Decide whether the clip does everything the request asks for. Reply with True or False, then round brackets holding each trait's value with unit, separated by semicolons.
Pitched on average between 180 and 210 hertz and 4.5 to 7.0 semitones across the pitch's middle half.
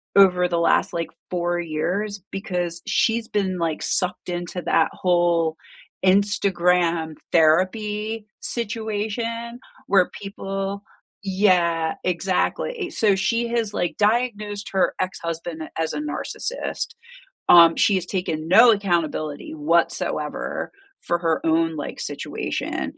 False (185 Hz; 3.6 semitones)